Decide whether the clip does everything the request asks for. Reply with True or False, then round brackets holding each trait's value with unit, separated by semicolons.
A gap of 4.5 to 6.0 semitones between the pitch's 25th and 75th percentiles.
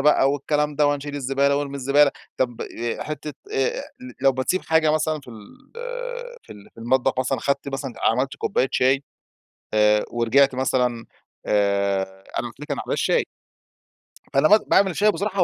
False (3.2 semitones)